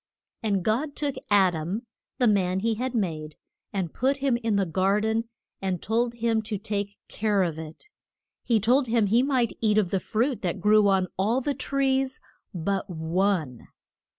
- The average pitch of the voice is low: No, high, 210 Hz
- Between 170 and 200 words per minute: Yes, average, 180 wpm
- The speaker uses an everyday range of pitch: Yes, average, 4.0 semitones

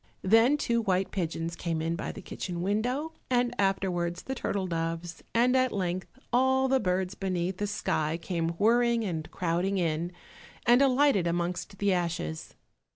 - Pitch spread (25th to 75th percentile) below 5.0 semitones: No, wide, 5.5 semitones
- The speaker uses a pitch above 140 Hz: Yes, high, 190 Hz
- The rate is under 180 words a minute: Yes, average, 155 wpm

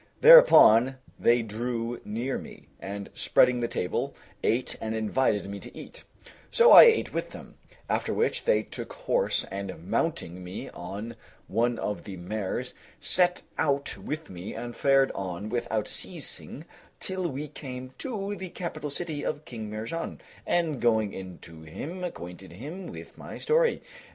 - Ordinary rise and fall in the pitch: No, wide, 7.7 semitones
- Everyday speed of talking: Yes, average, 155 wpm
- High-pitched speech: No, low, 120 Hz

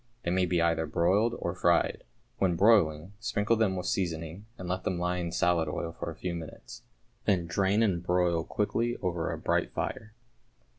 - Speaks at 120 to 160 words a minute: No, average, 185 wpm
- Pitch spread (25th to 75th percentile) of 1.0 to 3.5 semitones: Yes, average, 2.8 semitones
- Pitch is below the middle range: Yes, very low, 90 Hz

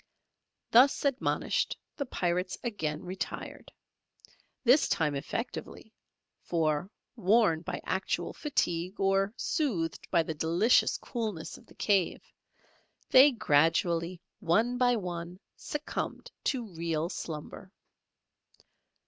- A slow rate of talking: Yes, slow, 100 wpm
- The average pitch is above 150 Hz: Yes, medium, 185 Hz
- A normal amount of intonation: No, wide, 6.2 semitones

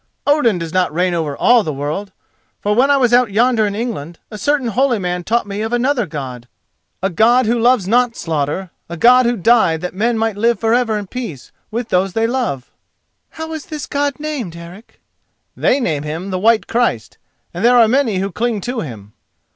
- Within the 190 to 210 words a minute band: Yes, fast, 205 wpm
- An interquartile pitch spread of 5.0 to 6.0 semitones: Yes, wide, 5.5 semitones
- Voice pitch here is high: Yes, high, 220 Hz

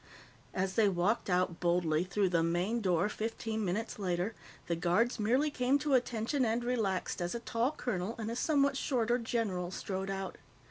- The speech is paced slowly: No, average, 175 wpm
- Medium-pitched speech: No, high, 215 Hz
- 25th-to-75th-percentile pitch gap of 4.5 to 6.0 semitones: Yes, average, 4.8 semitones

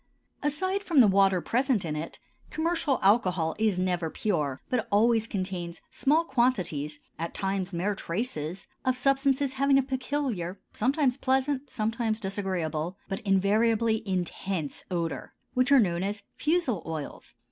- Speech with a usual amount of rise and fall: No, wide, 6.5 semitones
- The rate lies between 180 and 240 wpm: No, slow, 135 wpm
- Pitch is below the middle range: No, high, 210 Hz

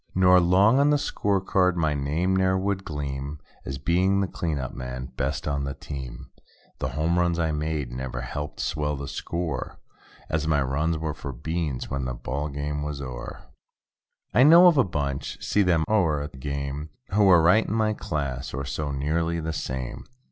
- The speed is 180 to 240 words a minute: Yes, average, 185 wpm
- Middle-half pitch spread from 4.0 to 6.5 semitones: Yes, average, 4.5 semitones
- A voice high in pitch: No, very low, 75 Hz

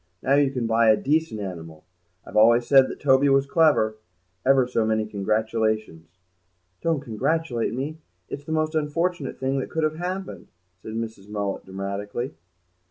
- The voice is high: No, low, 125 Hz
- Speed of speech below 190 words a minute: Yes, average, 160 wpm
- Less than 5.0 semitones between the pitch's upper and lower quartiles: No, wide, 5.4 semitones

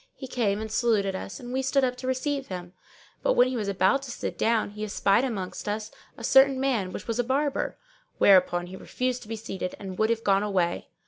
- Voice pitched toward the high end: Yes, high, 225 Hz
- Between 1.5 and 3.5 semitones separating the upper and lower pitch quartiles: No, average, 4.6 semitones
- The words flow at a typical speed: No, fast, 230 wpm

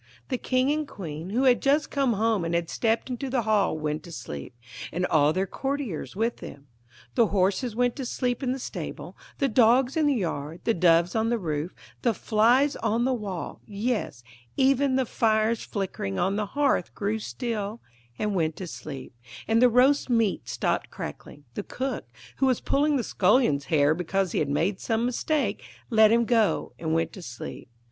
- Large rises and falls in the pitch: Yes, wide, 6.1 semitones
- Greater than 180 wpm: Yes, average, 190 wpm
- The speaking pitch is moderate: No, high, 220 Hz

